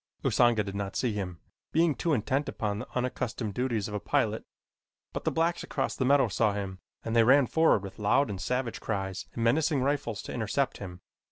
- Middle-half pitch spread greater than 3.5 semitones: Yes, average, 5.0 semitones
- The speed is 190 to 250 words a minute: Yes, average, 200 wpm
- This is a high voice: No, low, 115 Hz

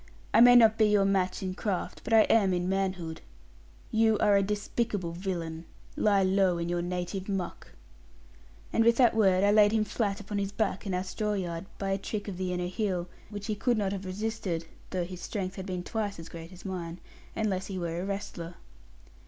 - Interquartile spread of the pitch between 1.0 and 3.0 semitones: Yes, narrow, 2.6 semitones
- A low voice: No, high, 195 Hz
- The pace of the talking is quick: Yes, fast, 210 wpm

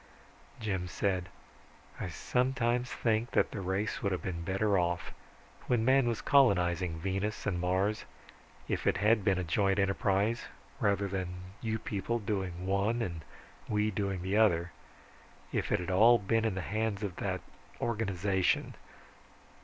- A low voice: Yes, low, 100 Hz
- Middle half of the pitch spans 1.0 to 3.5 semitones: Yes, average, 2.9 semitones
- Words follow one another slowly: No, average, 145 wpm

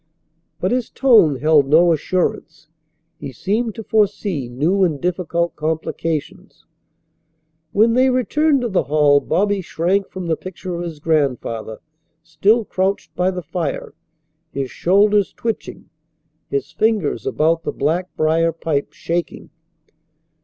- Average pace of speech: No, slow, 130 wpm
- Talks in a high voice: No, medium, 170 Hz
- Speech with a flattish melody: No, average, 4.6 semitones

